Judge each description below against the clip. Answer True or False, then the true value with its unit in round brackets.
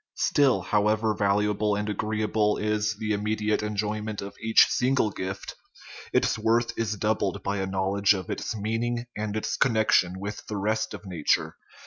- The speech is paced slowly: False (155 wpm)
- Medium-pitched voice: False (105 Hz)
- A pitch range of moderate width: False (1.4 semitones)